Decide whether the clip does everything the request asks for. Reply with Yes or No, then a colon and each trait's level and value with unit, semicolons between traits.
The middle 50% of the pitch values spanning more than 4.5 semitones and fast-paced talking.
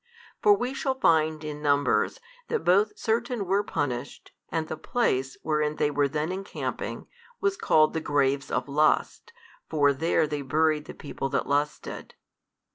No: average, 5.2 semitones; average, 155 wpm